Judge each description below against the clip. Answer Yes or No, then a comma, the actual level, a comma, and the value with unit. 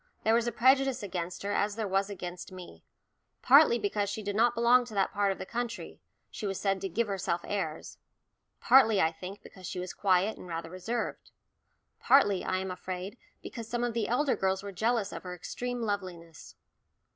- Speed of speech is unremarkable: Yes, average, 195 wpm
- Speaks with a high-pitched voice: Yes, high, 200 Hz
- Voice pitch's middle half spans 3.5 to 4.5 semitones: Yes, average, 4.1 semitones